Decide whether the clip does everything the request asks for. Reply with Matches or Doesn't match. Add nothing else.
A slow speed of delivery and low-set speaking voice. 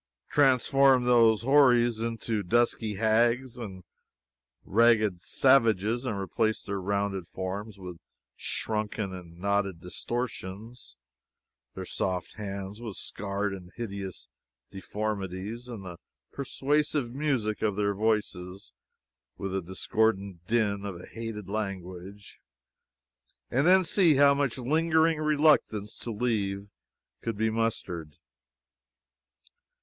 Matches